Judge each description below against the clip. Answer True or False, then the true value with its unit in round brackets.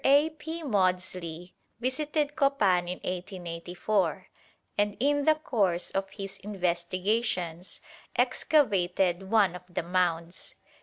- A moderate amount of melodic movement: False (6.1 semitones)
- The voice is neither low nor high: False (195 Hz)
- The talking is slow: True (105 wpm)